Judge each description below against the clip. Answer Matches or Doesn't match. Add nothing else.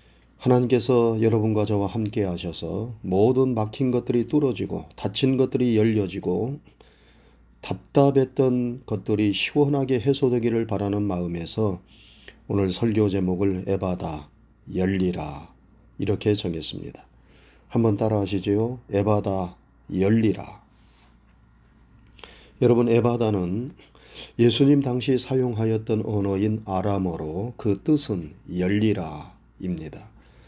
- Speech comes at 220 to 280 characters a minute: Matches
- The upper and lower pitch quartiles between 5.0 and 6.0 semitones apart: Doesn't match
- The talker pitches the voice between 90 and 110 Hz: Matches